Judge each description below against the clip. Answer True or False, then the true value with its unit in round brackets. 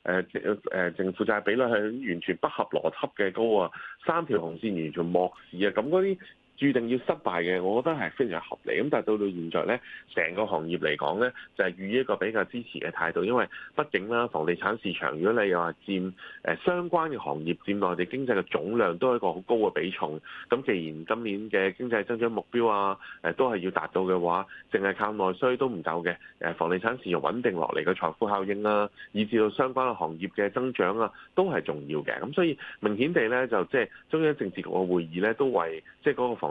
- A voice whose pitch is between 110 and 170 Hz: False (100 Hz)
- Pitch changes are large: False (4.8 semitones)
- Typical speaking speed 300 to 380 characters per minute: True (330 characters per minute)